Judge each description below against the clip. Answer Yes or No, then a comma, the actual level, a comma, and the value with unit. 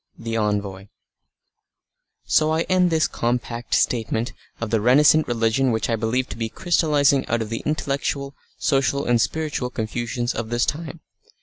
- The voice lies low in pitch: Yes, low, 120 Hz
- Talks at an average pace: Yes, average, 150 wpm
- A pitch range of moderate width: Yes, average, 4.2 semitones